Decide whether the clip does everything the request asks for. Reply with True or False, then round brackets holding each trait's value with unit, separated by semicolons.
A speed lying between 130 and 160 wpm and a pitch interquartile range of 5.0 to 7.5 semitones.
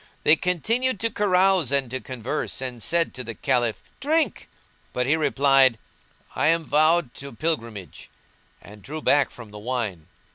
True (155 wpm; 5.6 semitones)